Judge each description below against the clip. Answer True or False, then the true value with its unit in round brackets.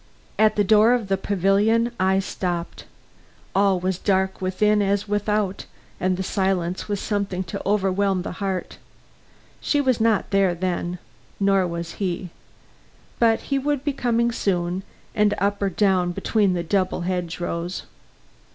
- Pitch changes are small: True (2.3 semitones)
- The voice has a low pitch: False (195 Hz)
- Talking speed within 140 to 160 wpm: True (150 wpm)